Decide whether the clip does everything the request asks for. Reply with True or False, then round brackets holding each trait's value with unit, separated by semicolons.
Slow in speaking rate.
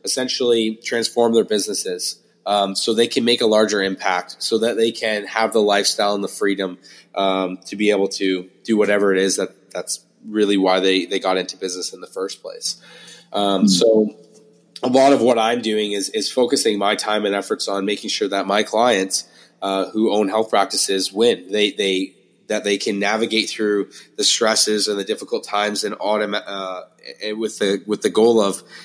False (195 wpm)